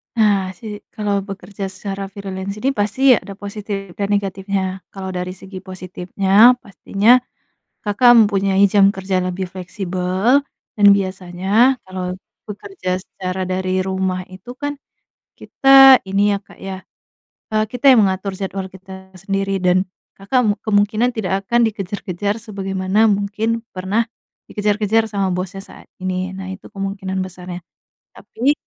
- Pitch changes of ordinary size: No, narrow, 1.9 semitones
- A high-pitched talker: Yes, high, 195 Hz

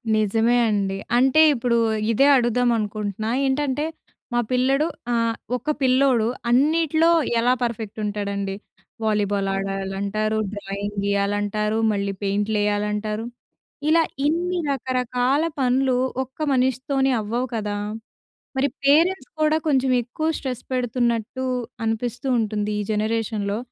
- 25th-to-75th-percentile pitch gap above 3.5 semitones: Yes, average, 4.1 semitones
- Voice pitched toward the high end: Yes, high, 230 Hz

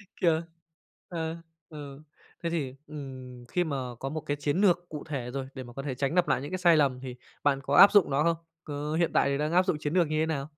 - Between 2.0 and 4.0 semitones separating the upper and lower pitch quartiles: Yes, average, 3.3 semitones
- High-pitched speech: No, medium, 150 Hz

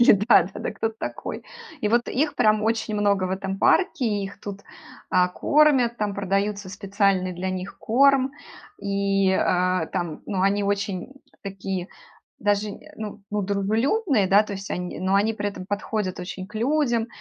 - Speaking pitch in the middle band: No, high, 200 Hz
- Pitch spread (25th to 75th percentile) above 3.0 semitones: No, narrow, 2.4 semitones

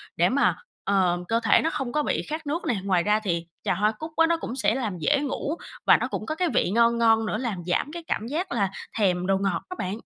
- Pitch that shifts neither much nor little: No, wide, 7.1 semitones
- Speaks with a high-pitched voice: Yes, high, 225 Hz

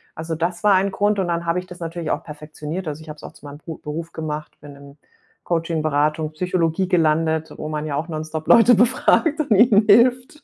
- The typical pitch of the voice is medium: Yes, medium, 165 Hz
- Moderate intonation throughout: Yes, average, 3.5 semitones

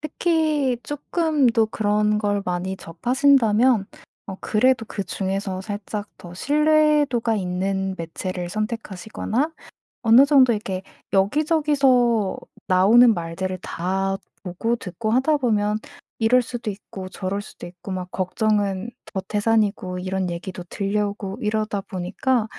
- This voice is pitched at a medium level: No, high, 210 Hz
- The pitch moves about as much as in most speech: Yes, average, 4.3 semitones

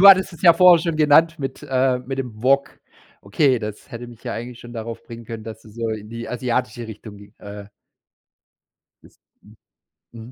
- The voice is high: No, low, 120 Hz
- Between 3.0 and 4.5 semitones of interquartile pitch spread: Yes, average, 3.8 semitones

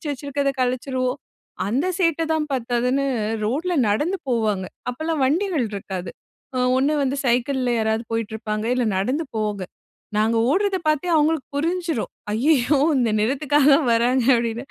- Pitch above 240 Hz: Yes, very high, 260 Hz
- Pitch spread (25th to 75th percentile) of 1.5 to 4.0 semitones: No, average, 4.8 semitones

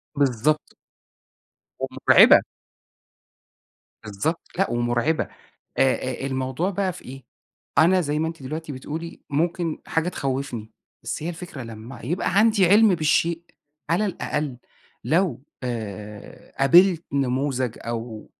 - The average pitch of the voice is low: No, medium, 145 Hz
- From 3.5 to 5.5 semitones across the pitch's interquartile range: Yes, average, 5.1 semitones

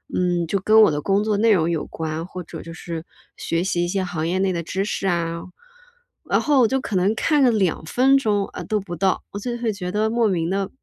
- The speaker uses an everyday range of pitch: Yes, average, 4.0 semitones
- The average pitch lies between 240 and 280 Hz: No, high, 190 Hz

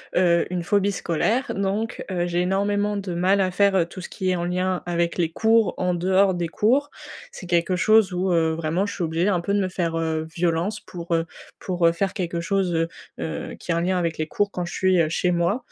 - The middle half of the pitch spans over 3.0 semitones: No, narrow, 2.6 semitones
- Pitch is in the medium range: Yes, medium, 180 Hz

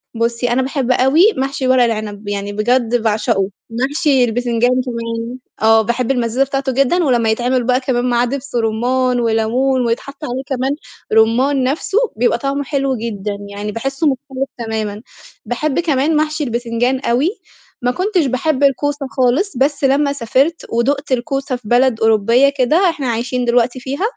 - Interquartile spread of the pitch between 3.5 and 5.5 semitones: No, average, 2.9 semitones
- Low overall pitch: No, very high, 255 Hz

